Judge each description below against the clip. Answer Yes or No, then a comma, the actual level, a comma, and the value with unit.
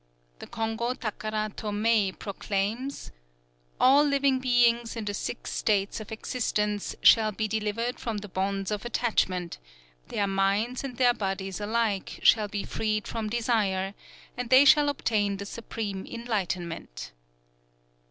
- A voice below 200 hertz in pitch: No, high, 215 Hz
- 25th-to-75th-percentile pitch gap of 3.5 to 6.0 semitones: No, average, 3.0 semitones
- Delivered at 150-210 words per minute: No, average, 140 wpm